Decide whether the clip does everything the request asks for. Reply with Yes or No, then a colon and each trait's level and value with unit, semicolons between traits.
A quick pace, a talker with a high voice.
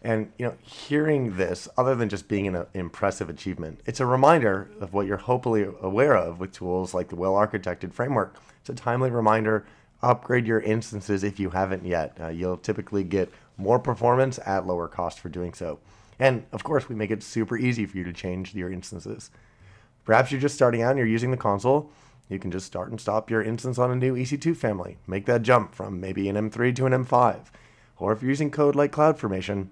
No: fast, 210 wpm; low, 110 Hz